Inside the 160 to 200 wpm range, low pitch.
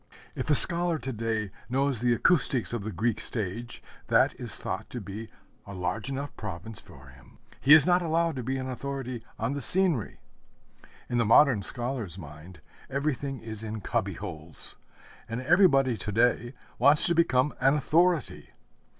Yes: average, 165 wpm; low, 125 Hz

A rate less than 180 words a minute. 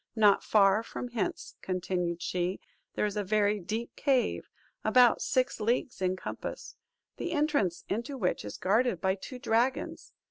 Yes: average, 150 wpm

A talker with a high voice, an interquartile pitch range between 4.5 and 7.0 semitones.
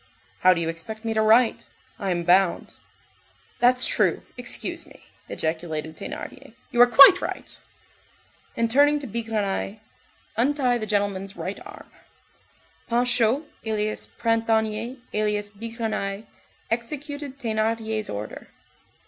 No: high, 220 Hz; average, 3.2 semitones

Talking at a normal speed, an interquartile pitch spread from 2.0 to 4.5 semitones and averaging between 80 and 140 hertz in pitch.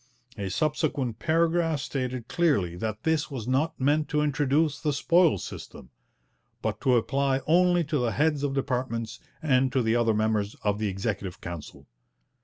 No: average, 160 wpm; average, 5.3 semitones; low, 135 Hz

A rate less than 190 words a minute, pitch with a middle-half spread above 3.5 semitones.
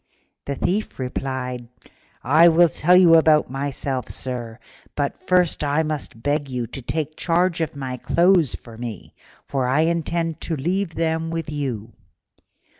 Yes: average, 150 wpm; average, 4.2 semitones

